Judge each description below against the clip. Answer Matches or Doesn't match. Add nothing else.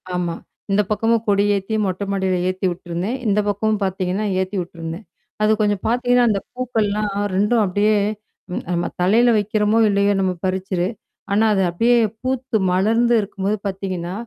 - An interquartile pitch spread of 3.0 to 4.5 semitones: Doesn't match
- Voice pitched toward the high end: Matches